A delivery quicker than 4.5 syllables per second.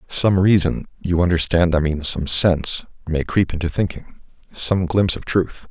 Yes: 4.8 syllables/s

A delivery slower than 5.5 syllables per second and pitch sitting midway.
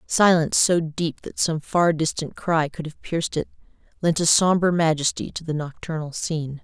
Yes: 5.0 syllables/s; medium, 160 Hz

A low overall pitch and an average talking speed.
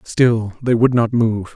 Yes: low, 115 Hz; average, 195 wpm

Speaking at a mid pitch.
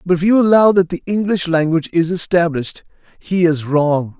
Yes: medium, 170 Hz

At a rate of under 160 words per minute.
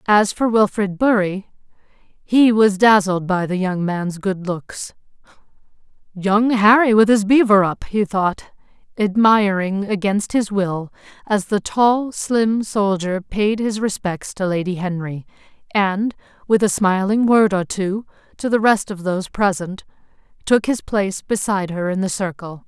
Yes: average, 150 wpm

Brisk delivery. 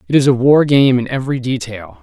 Yes: fast, 235 wpm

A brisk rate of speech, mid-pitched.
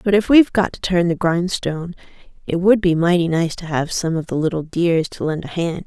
Yes: fast, 245 wpm; medium, 170 Hz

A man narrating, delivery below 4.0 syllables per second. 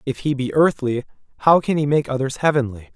No: male; 5.9 syllables/s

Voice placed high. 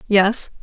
Yes: high, 210 Hz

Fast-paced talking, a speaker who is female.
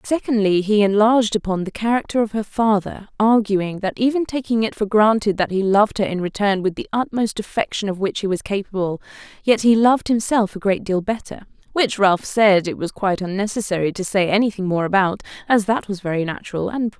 Yes: fast, 210 wpm; female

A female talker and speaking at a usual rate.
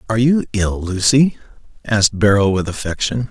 No: male; average, 145 wpm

